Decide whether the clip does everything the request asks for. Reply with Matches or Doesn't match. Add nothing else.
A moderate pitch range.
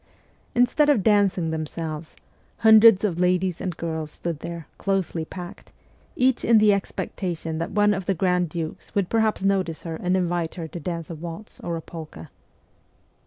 Matches